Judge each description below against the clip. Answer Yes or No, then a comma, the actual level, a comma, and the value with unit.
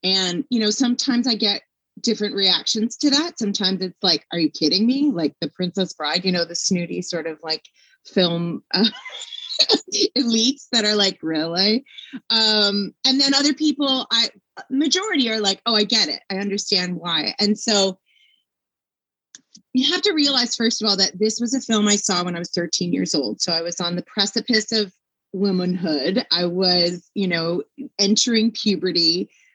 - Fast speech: No, average, 175 wpm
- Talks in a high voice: Yes, high, 210 Hz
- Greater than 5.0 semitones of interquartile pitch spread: Yes, wide, 5.6 semitones